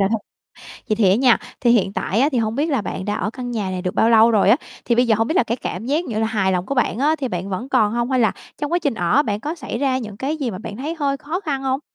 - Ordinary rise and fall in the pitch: Yes, average, 4.5 semitones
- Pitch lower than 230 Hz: No, high, 235 Hz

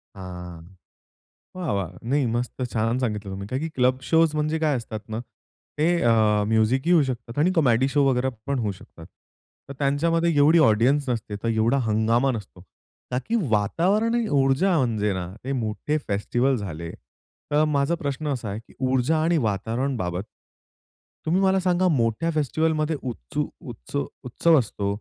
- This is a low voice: Yes, low, 130 Hz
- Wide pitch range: Yes, wide, 6.0 semitones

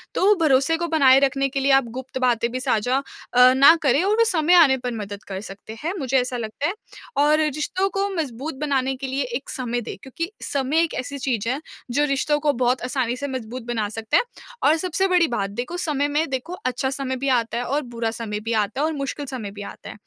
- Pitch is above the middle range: Yes, very high, 270 Hz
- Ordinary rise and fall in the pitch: Yes, average, 3.6 semitones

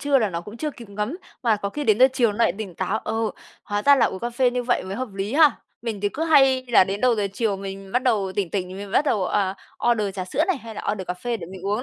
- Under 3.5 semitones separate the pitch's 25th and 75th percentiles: No, average, 4.2 semitones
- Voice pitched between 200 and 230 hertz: Yes, high, 215 Hz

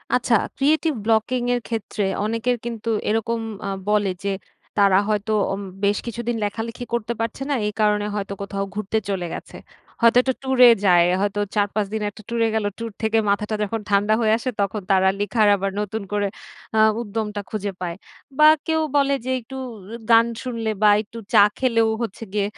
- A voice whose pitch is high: Yes, high, 220 Hz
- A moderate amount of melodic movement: No, narrow, 2.3 semitones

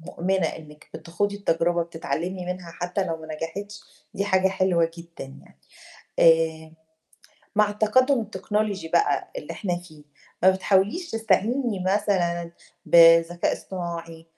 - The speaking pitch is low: No, medium, 180 Hz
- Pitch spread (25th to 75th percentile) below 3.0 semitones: No, average, 3.4 semitones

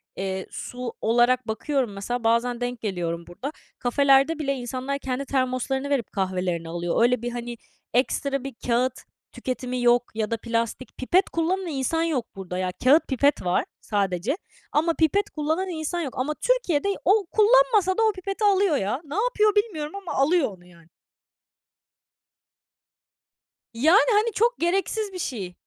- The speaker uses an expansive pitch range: Yes, wide, 6.7 semitones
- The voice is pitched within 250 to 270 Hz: Yes, very high, 265 Hz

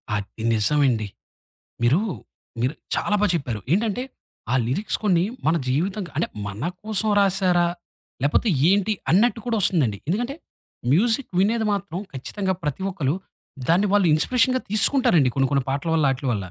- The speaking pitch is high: No, medium, 175 Hz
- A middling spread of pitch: No, wide, 7.2 semitones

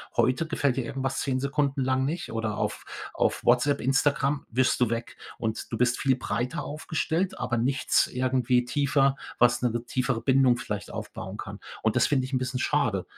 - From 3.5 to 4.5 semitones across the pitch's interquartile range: No, narrow, 2.4 semitones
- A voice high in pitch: No, low, 130 Hz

